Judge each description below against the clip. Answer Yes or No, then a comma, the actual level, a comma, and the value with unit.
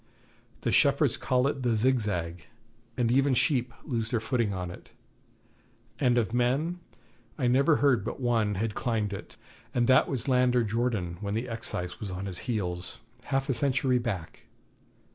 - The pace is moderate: Yes, average, 160 wpm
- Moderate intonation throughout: Yes, average, 3.8 semitones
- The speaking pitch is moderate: No, low, 120 Hz